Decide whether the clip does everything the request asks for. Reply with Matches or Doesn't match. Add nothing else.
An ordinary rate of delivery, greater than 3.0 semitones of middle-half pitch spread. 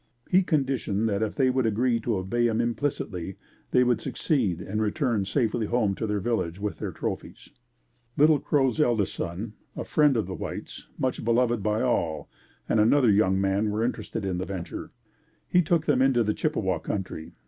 Matches